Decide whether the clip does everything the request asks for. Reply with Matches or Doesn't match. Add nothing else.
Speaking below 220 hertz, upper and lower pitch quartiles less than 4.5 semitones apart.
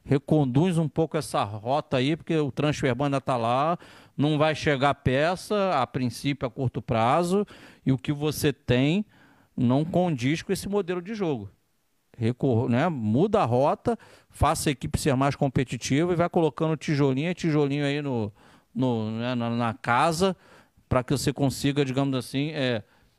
Matches